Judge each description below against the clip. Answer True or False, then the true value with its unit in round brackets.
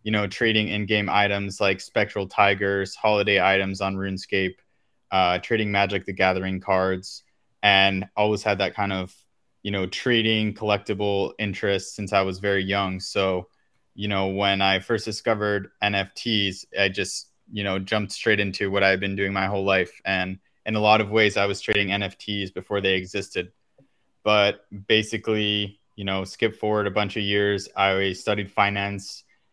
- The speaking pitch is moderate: False (100 Hz)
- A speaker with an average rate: True (170 wpm)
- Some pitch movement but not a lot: False (1.5 semitones)